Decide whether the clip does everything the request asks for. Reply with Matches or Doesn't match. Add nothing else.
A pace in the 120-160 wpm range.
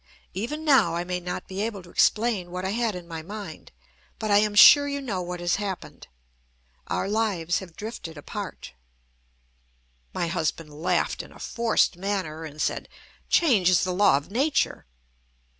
Doesn't match